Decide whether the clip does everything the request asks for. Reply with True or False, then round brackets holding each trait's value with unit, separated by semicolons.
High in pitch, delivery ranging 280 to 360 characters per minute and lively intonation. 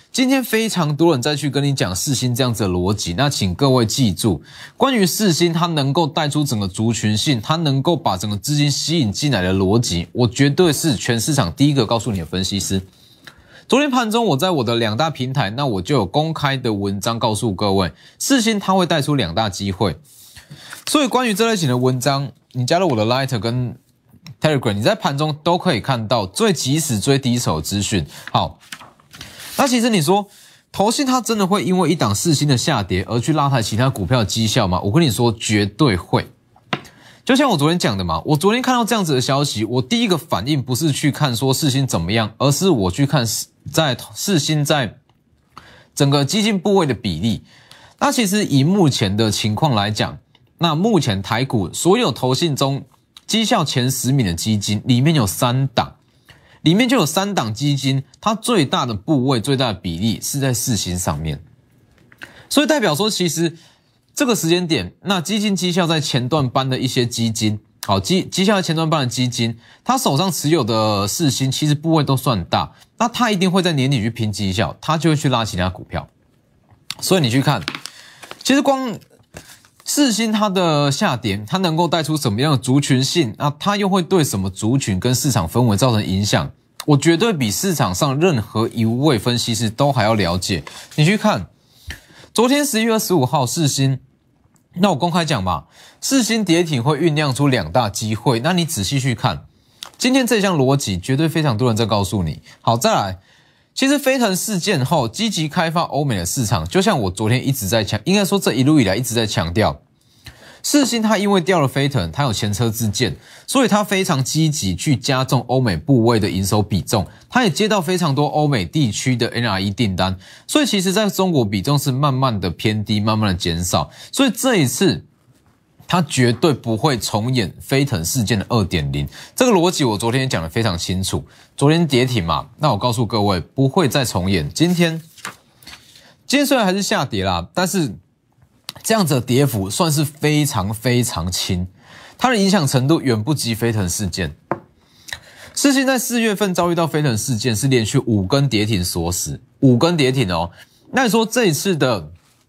False (135 Hz; 285 characters per minute; 7.1 semitones)